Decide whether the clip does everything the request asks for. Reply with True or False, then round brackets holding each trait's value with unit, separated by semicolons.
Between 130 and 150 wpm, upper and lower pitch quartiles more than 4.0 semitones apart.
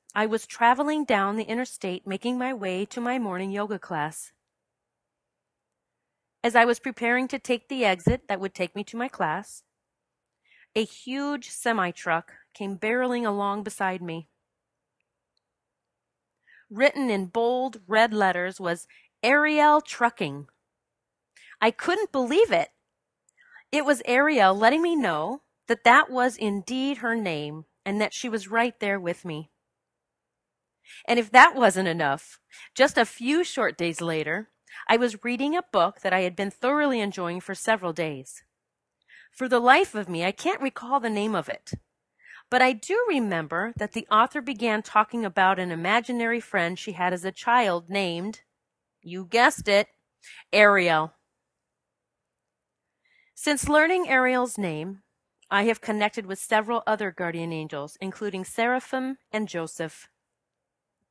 True (145 wpm; 5.1 semitones)